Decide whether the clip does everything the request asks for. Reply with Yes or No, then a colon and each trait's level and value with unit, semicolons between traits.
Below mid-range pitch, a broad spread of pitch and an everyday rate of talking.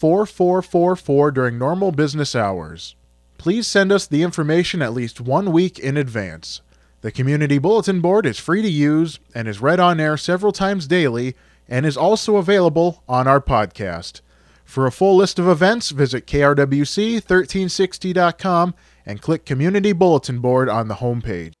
No: medium, 150 Hz; wide, 6.8 semitones; average, 155 wpm